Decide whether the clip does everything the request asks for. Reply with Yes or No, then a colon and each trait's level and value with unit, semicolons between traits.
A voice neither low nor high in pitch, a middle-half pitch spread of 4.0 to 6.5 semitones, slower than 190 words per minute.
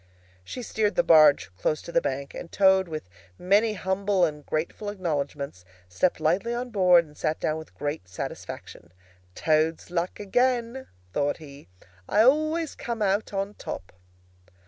Yes: medium, 180 Hz; wide, 5.5 semitones; average, 150 wpm